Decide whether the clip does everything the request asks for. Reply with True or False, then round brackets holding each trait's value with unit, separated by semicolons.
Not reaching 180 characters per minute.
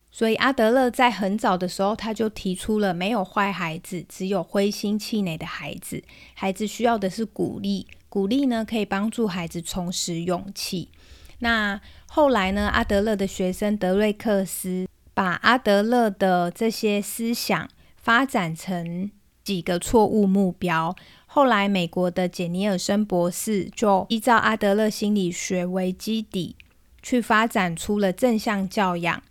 False (235 characters per minute)